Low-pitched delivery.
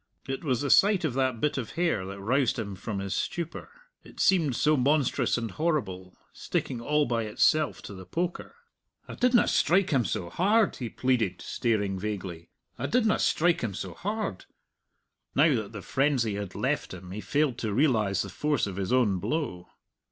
Yes: low, 125 Hz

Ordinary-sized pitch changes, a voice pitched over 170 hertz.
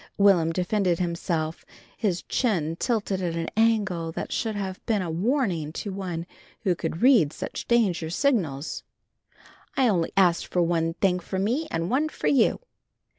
Yes: average, 4.7 semitones; medium, 185 Hz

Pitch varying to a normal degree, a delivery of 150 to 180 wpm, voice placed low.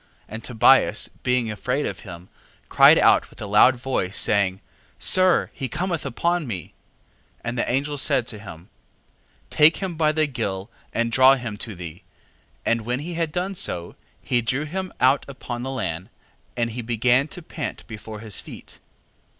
No: wide, 5.8 semitones; average, 175 wpm; low, 125 Hz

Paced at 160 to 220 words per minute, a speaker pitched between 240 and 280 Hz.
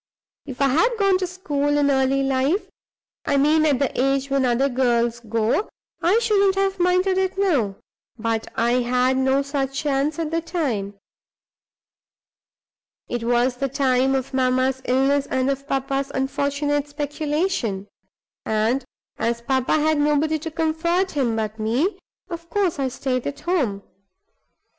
No: average, 150 wpm; very high, 275 Hz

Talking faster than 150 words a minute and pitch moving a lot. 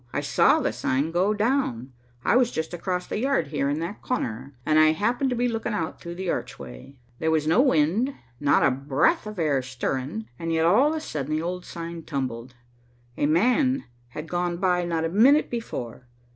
Yes: average, 200 wpm; wide, 7.0 semitones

